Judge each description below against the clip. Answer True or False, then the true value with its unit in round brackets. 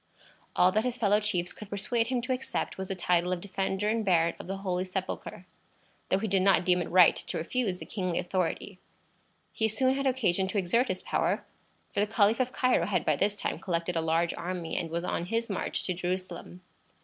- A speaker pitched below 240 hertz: True (190 Hz)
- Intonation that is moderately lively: True (3.3 semitones)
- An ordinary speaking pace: False (215 wpm)